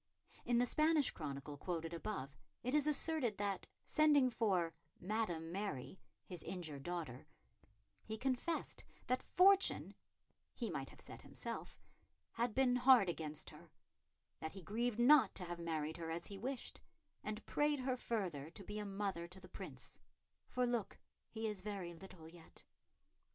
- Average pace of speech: Yes, average, 155 wpm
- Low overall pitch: No, high, 200 Hz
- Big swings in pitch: Yes, wide, 6.7 semitones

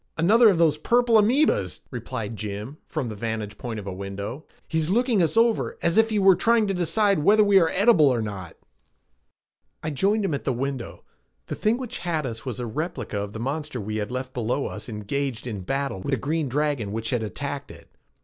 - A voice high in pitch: No, medium, 140 Hz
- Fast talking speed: Yes, fast, 210 wpm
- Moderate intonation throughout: No, wide, 9.0 semitones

